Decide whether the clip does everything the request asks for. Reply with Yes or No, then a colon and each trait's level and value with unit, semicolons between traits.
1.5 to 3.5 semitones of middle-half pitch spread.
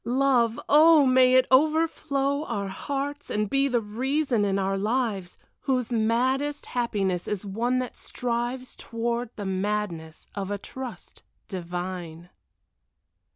No: average, 4.9 semitones